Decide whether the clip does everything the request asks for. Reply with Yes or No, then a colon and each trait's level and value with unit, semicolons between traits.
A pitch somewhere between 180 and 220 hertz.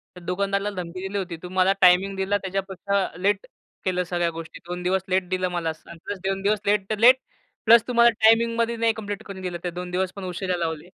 Yes: high, 190 Hz